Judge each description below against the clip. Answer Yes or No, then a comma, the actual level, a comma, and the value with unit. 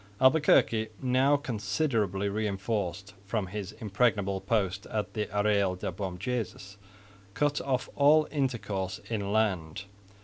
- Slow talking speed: Yes, slow, 110 wpm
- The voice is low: Yes, low, 105 Hz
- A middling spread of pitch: Yes, average, 4.1 semitones